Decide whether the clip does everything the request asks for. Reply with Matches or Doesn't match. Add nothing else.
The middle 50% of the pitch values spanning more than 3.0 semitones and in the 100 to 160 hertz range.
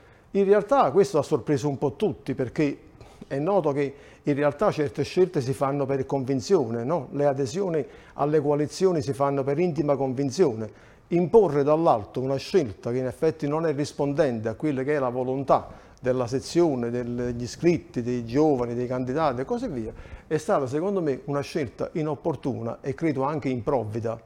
Matches